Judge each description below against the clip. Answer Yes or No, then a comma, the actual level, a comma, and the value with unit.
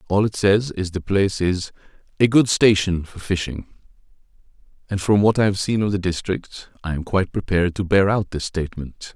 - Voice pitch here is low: Yes, very low, 95 Hz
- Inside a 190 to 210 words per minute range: Yes, average, 195 wpm